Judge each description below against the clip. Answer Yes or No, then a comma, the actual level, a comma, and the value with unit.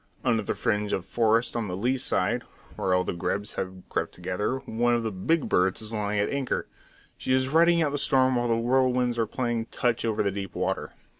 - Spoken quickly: Yes, fast, 220 wpm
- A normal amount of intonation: Yes, average, 3.9 semitones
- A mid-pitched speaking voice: No, low, 115 Hz